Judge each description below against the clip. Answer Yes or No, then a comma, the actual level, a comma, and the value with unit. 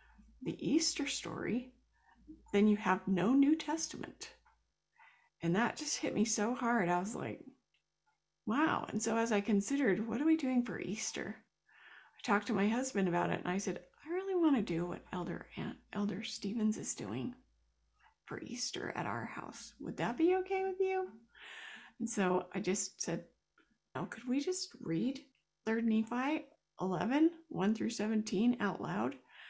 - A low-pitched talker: No, high, 225 Hz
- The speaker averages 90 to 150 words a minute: No, average, 165 wpm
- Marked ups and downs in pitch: Yes, wide, 6.3 semitones